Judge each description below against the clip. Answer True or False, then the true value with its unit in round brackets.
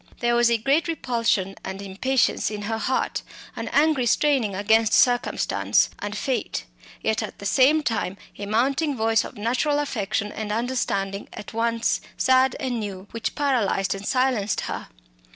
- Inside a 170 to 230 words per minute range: False (155 wpm)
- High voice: True (230 Hz)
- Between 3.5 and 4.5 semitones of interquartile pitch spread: True (4.0 semitones)